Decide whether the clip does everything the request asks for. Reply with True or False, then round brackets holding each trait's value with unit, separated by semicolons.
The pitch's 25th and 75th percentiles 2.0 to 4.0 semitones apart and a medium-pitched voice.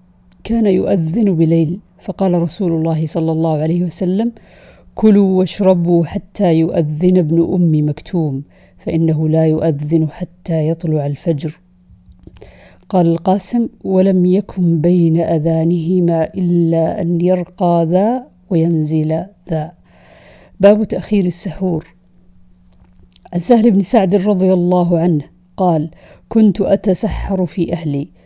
True (2.8 semitones; 170 Hz)